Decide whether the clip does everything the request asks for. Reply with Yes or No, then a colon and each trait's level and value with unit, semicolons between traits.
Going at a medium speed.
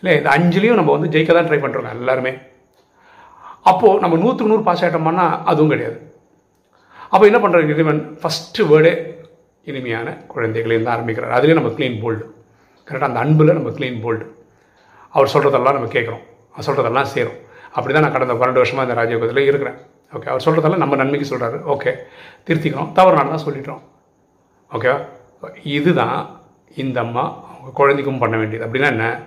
No: fast, 155 wpm